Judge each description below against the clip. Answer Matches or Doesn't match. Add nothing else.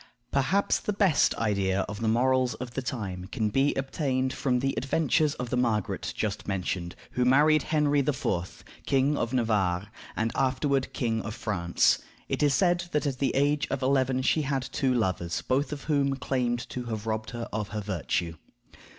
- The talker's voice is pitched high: Doesn't match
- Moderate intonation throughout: Matches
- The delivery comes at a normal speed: Matches